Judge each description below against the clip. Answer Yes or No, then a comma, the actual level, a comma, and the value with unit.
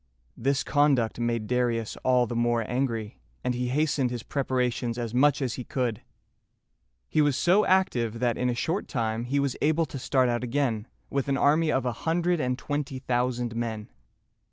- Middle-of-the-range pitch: No, low, 125 Hz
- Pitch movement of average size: Yes, average, 3.0 semitones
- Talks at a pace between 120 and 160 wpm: No, average, 180 wpm